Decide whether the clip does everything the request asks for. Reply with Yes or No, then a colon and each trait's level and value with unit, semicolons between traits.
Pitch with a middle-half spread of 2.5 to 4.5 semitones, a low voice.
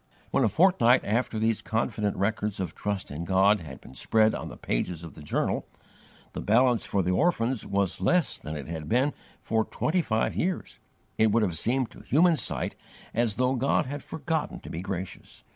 No: wide, 5.4 semitones; low, 110 Hz